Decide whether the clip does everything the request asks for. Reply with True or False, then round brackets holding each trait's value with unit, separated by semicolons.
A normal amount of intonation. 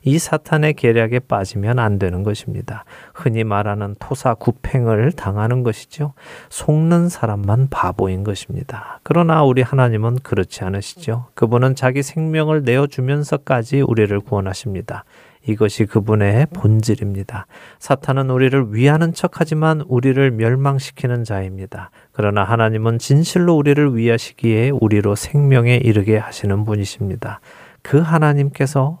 True (4.8 semitones)